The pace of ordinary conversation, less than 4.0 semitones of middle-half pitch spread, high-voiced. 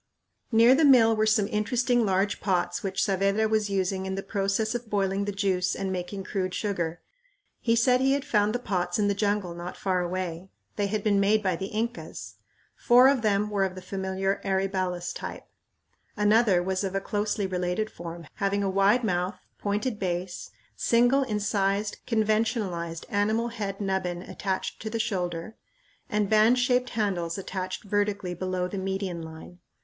Yes: average, 170 wpm; narrow, 2.6 semitones; high, 200 Hz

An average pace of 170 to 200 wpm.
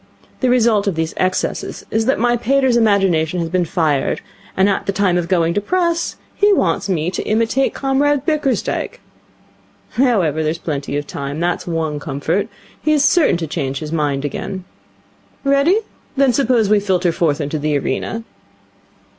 No: average, 160 wpm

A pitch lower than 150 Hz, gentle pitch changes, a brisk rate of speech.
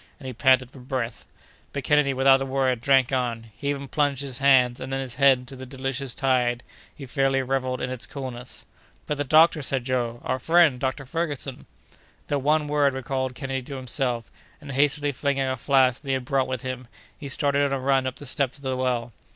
Yes: low, 135 Hz; narrow, 1.5 semitones; fast, 210 wpm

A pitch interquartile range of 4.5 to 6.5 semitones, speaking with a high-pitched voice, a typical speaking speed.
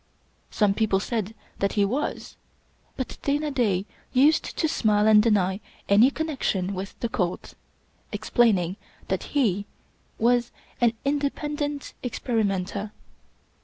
No: wide, 5.5 semitones; high, 220 Hz; slow, 125 wpm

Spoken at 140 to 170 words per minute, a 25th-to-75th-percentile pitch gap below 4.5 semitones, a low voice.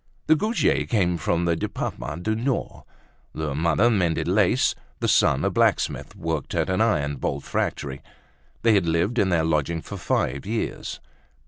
No: average, 160 wpm; average, 5.3 semitones; very low, 85 Hz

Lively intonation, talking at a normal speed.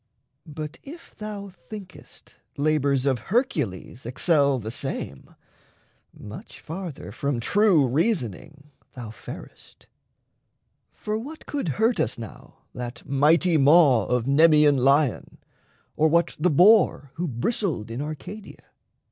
No: wide, 6.0 semitones; slow, 115 wpm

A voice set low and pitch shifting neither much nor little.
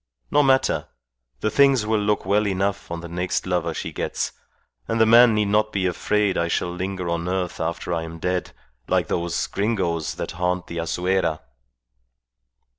Yes: very low, 95 Hz; average, 3.6 semitones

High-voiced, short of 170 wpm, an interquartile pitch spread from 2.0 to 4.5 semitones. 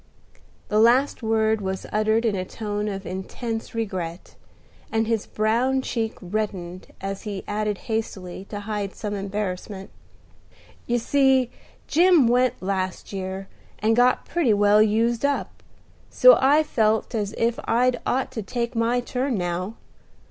Yes: high, 220 Hz; average, 140 wpm; average, 3.4 semitones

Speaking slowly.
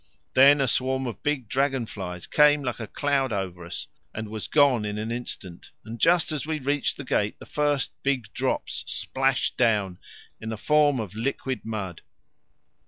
No: average, 175 wpm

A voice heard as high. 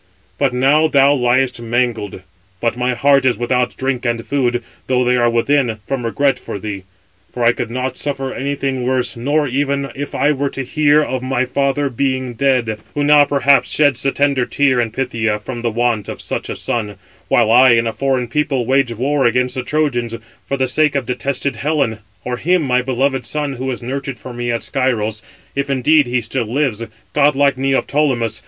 No: low, 130 Hz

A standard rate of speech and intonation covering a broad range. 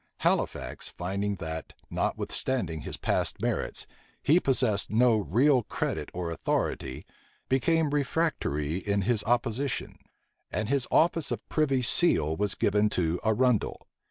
No: slow, 125 wpm; wide, 6.5 semitones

